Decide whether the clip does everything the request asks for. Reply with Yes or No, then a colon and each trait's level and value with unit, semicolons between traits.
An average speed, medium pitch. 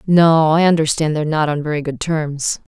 Yes: average, 195 wpm; medium, 155 Hz